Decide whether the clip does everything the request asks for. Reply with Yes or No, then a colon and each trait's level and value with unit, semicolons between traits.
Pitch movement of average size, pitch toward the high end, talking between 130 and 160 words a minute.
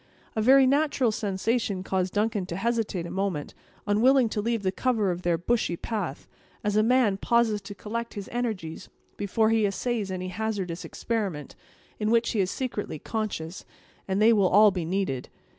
No: average, 3.5 semitones; high, 210 Hz; average, 170 wpm